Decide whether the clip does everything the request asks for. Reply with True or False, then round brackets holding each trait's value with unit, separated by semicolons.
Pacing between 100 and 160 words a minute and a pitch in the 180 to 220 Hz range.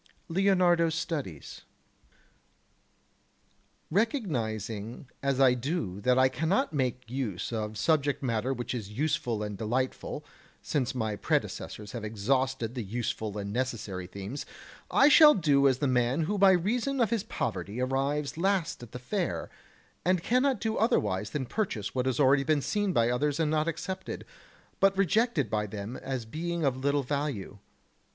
False (155 wpm; 135 Hz)